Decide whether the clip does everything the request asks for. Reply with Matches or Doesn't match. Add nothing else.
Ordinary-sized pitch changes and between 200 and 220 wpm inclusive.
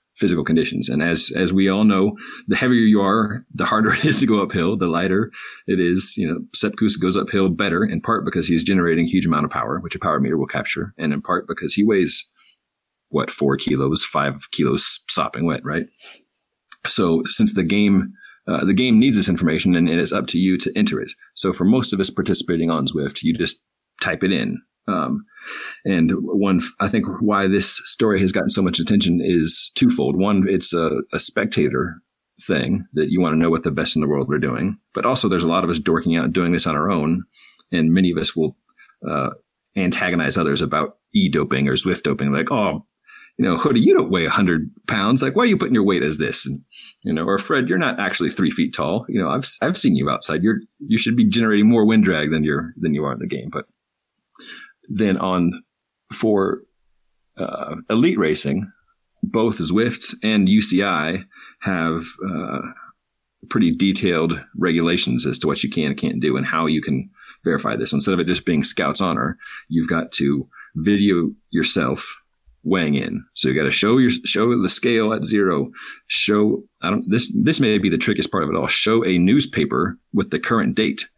Doesn't match